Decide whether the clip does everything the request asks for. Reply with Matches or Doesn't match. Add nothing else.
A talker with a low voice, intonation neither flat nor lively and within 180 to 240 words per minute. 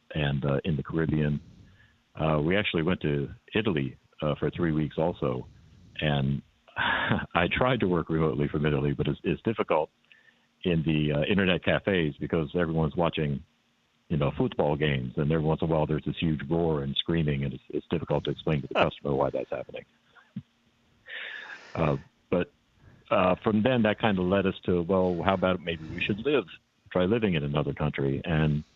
Matches